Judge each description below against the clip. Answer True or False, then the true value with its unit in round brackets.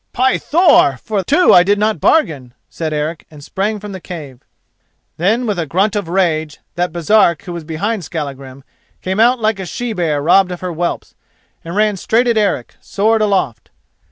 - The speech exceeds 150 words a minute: True (185 wpm)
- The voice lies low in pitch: False (185 Hz)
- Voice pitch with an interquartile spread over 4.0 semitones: True (5.3 semitones)